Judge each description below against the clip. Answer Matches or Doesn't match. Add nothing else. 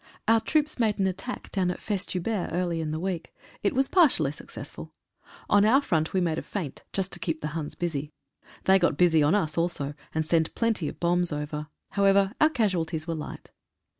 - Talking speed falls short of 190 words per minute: Doesn't match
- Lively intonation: Doesn't match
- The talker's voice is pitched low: Doesn't match